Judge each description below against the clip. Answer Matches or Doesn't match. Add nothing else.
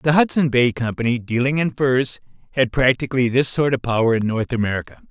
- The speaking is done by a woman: Doesn't match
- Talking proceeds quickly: Doesn't match